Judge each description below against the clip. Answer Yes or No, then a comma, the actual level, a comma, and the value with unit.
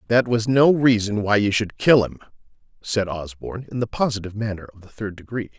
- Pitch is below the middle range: Yes, low, 110 Hz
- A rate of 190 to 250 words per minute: Yes, fast, 205 wpm